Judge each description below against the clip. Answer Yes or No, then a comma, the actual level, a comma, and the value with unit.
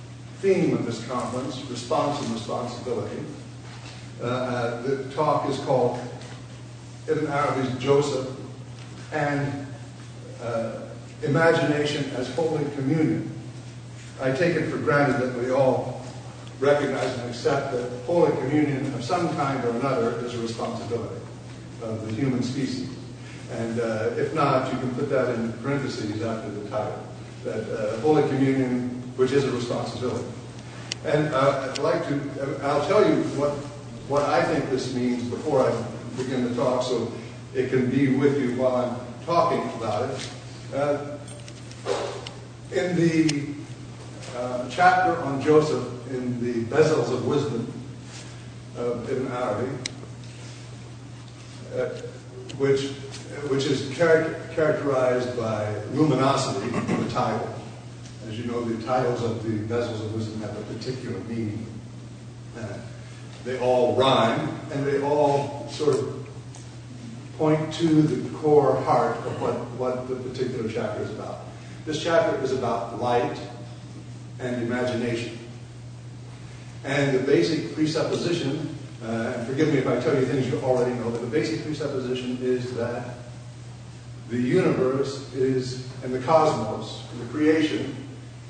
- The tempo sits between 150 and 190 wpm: No, slow, 135 wpm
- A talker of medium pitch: No, low, 125 Hz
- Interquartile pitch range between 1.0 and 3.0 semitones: Yes, narrow, 2.4 semitones